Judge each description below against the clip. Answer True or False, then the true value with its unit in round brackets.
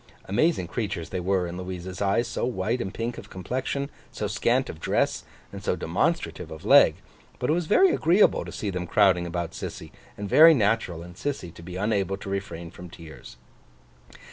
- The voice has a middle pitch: False (100 Hz)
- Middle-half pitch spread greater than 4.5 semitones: True (5.2 semitones)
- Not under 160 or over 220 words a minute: True (190 wpm)